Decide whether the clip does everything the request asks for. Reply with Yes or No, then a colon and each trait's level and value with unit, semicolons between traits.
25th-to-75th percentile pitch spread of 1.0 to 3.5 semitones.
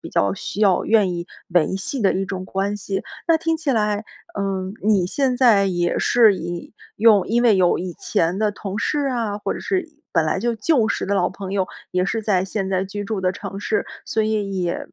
Yes: average, 2.9 semitones